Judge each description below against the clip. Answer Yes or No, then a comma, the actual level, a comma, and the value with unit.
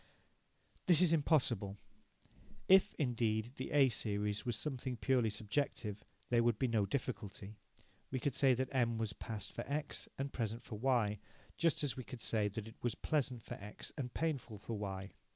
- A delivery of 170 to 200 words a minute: Yes, average, 175 wpm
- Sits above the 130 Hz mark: No, low, 120 Hz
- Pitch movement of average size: Yes, average, 4.1 semitones